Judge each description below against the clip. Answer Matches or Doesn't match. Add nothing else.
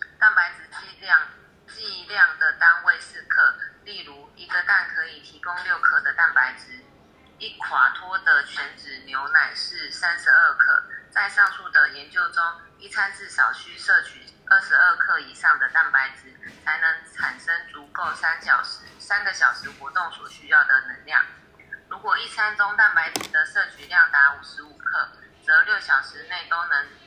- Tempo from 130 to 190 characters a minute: Doesn't match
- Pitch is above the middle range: Matches